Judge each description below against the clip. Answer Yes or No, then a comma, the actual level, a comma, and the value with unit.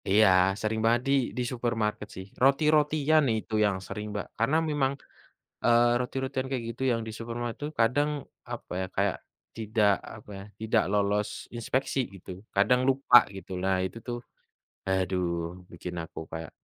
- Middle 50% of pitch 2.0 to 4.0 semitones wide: No, average, 4.5 semitones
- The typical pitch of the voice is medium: No, low, 115 Hz